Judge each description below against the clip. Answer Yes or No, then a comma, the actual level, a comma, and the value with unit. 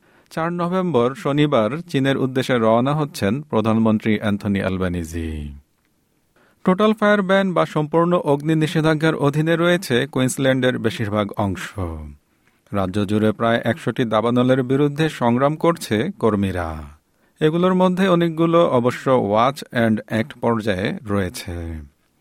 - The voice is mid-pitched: No, low, 125 Hz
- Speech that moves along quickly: No, average, 110 wpm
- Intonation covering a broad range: Yes, wide, 7.4 semitones